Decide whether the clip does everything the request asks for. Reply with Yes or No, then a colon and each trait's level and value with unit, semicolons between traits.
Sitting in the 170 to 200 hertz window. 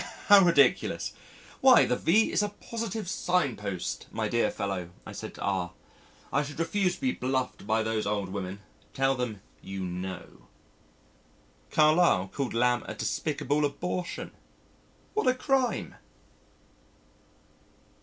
No: low, 130 Hz